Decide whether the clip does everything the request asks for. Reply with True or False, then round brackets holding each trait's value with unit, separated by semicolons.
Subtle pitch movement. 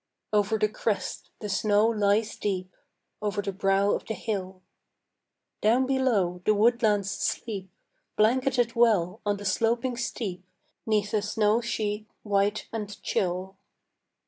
True (2.3 semitones)